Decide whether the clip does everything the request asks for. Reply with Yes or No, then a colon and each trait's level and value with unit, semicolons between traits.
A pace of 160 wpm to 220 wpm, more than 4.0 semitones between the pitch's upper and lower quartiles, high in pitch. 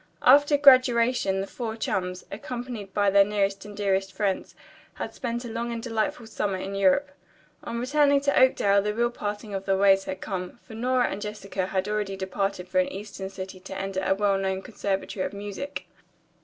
No: average, 190 wpm; average, 3.6 semitones; high, 205 Hz